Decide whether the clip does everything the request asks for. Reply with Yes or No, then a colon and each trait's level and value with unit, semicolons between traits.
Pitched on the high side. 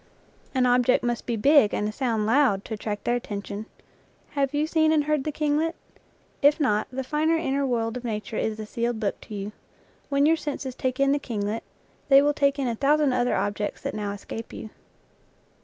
Yes: very high, 250 Hz